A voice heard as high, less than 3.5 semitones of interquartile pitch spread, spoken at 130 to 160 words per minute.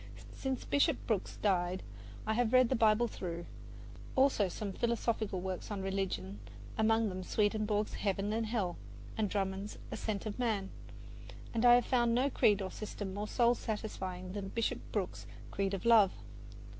Yes: high, 210 Hz; average, 3.1 semitones; average, 155 wpm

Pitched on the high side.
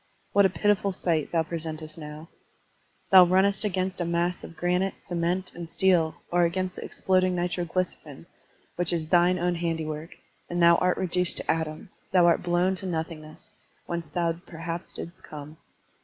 No: medium, 175 Hz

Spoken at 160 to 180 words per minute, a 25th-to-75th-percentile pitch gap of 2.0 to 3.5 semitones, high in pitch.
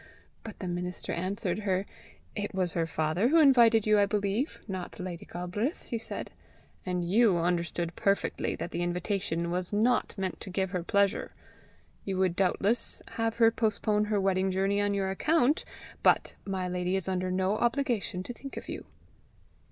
Yes: average, 170 wpm; average, 3.0 semitones; high, 195 Hz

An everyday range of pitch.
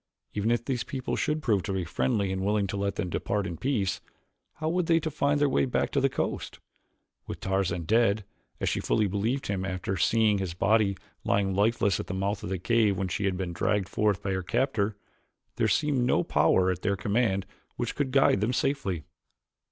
Yes: average, 3.9 semitones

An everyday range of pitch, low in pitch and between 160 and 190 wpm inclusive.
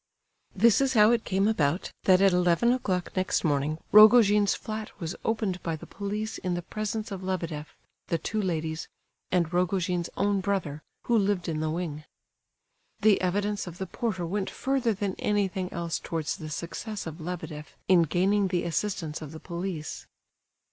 No: average, 3.6 semitones; medium, 185 Hz; average, 170 wpm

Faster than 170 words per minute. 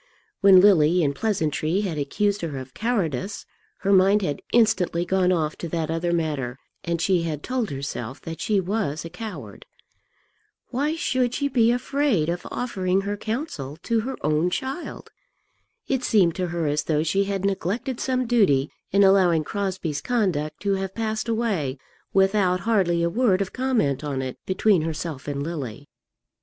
No: average, 165 wpm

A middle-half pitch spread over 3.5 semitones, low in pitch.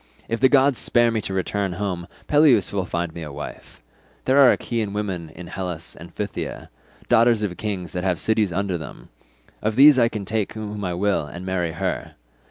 Yes: average, 3.9 semitones; low, 100 Hz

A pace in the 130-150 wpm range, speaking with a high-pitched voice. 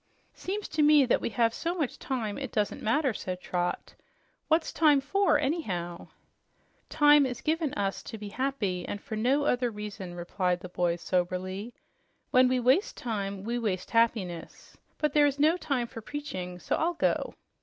No: average, 175 wpm; high, 235 Hz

